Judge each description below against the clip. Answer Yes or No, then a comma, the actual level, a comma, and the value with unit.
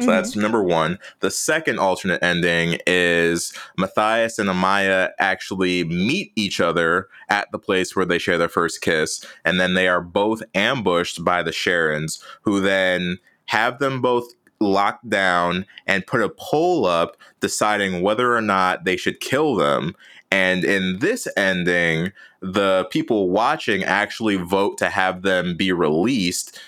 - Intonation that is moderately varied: No, narrow, 2.1 semitones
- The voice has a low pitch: Yes, very low, 95 Hz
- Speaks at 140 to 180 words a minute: Yes, average, 155 wpm